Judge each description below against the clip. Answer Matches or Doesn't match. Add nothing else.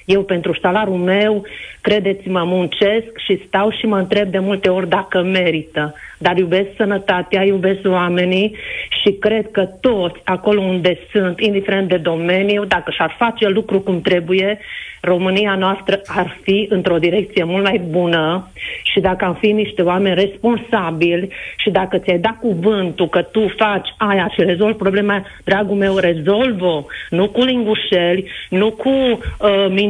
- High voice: Matches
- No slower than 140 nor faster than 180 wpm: Matches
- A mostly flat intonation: Matches